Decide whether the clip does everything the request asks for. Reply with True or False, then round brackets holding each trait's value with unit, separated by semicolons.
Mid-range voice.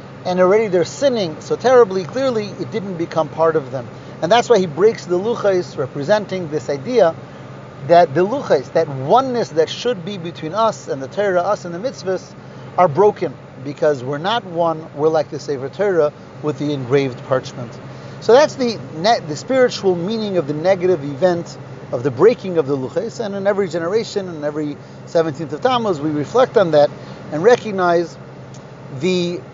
True (175 Hz)